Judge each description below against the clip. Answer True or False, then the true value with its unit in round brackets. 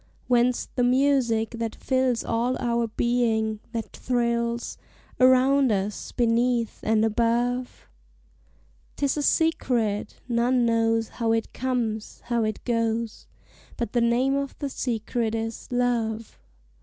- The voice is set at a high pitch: True (235 Hz)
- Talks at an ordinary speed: False (120 wpm)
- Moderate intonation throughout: False (1.8 semitones)